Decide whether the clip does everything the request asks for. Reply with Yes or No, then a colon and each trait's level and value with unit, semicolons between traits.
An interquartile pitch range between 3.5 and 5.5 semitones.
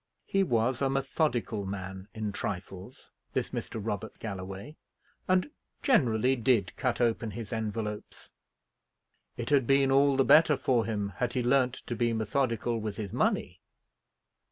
Yes: average, 4.1 semitones